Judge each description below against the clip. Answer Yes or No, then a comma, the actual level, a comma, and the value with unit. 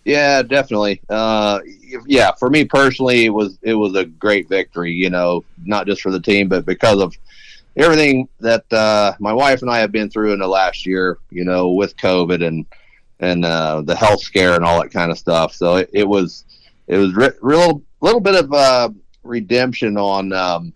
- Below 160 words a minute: No, average, 200 wpm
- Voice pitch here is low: Yes, low, 105 Hz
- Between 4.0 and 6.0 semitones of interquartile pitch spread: Yes, average, 4.7 semitones